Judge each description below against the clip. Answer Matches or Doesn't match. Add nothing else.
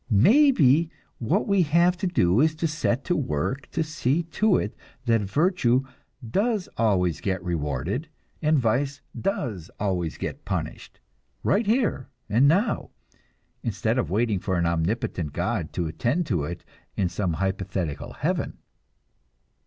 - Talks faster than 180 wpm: Doesn't match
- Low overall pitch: Matches